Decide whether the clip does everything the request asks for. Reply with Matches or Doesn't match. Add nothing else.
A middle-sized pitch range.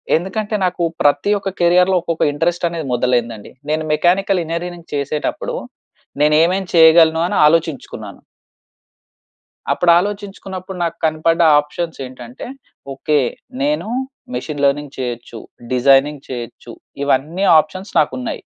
Matches